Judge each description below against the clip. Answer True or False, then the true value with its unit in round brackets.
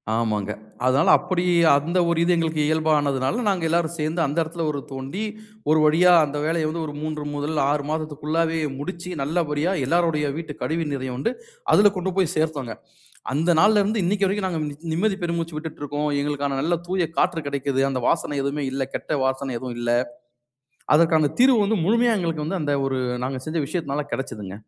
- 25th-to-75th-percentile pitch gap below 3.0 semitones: False (3.4 semitones)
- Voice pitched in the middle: True (155 Hz)